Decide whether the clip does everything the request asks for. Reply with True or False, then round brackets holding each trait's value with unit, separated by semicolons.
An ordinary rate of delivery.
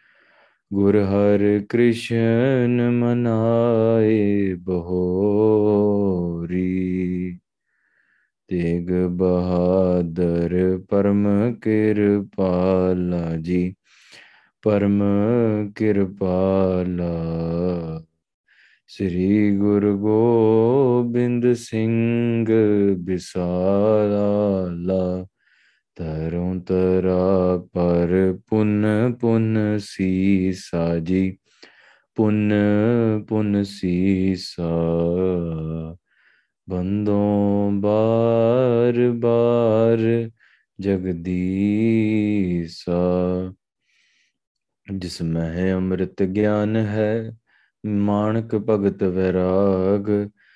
False (45 wpm)